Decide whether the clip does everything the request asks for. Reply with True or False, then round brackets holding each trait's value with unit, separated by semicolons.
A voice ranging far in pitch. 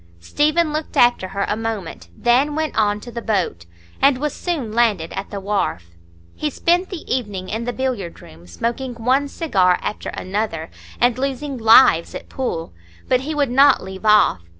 True (6.0 semitones)